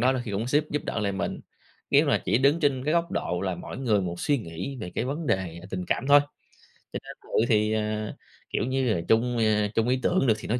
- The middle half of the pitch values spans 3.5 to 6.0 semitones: Yes, average, 4.7 semitones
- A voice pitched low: Yes, low, 115 Hz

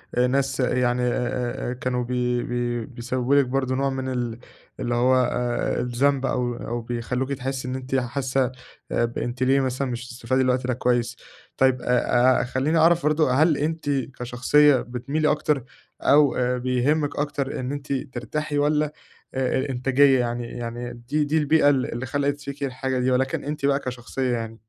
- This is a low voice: Yes, low, 130 Hz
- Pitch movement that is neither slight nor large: No, narrow, 2.3 semitones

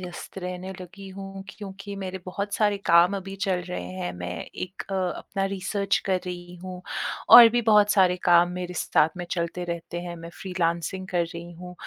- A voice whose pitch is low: No, medium, 185 Hz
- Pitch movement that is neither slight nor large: No, narrow, 1.9 semitones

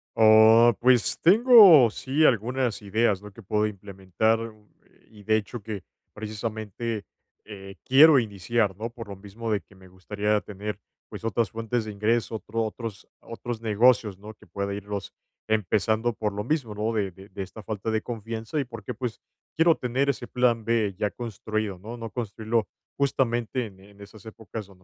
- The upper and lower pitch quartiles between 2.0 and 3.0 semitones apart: Yes, narrow, 2.4 semitones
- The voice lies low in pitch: Yes, low, 110 Hz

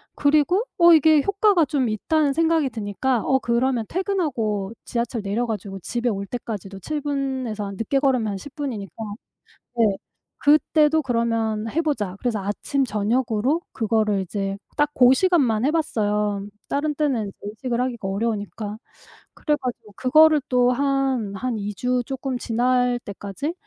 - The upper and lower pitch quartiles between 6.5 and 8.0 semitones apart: No, average, 5.1 semitones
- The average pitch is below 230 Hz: No, high, 245 Hz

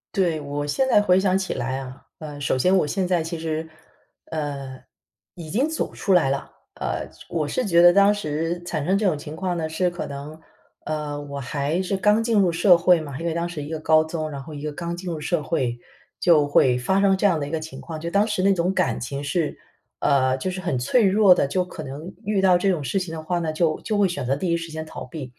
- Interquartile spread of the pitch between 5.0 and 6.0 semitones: No, average, 4.1 semitones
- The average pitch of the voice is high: No, medium, 165 Hz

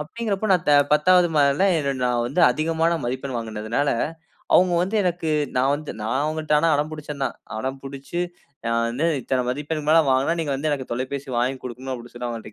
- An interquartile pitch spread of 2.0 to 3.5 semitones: No, average, 3.9 semitones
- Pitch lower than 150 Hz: Yes, medium, 140 Hz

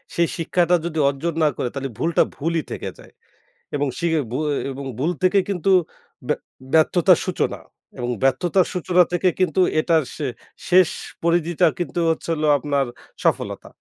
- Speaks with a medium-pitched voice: Yes, medium, 165 Hz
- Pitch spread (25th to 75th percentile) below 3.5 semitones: Yes, average, 3.0 semitones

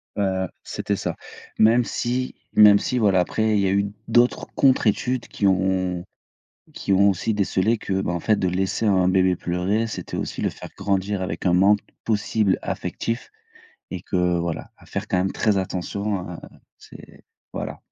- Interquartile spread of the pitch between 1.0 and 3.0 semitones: Yes, narrow, 2.6 semitones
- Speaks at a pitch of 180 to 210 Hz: No, low, 100 Hz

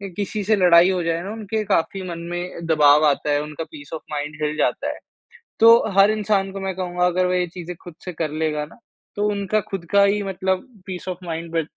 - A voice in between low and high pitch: Yes, medium, 180 Hz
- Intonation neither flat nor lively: Yes, average, 3.3 semitones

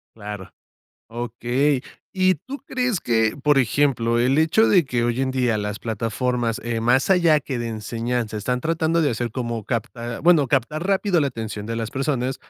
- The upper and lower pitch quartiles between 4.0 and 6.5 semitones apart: Yes, average, 4.5 semitones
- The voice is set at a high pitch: No, low, 125 Hz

